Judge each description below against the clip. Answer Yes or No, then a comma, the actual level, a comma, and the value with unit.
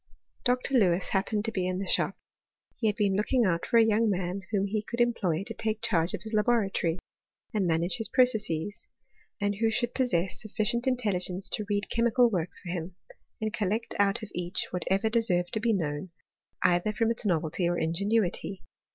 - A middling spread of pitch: Yes, average, 3.8 semitones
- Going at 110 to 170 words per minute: No, average, 190 wpm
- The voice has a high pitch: Yes, high, 205 Hz